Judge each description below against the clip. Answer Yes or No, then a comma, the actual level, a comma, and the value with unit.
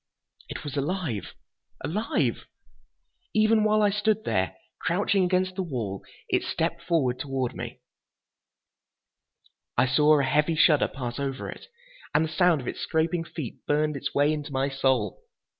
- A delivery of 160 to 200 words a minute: No, average, 150 wpm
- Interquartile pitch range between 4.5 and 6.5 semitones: Yes, average, 5.0 semitones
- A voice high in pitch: No, medium, 150 Hz